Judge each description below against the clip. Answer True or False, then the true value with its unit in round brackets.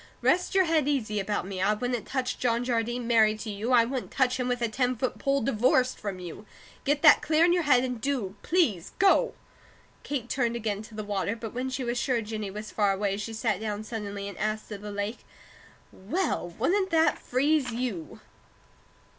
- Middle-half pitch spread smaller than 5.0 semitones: True (3.8 semitones)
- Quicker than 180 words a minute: True (205 wpm)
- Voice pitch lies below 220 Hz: False (235 Hz)